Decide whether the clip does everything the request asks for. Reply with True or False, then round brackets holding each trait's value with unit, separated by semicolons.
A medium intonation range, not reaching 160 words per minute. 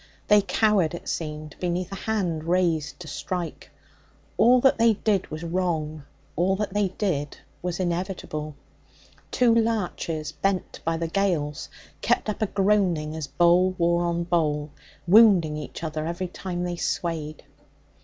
True (3.6 semitones; 145 wpm)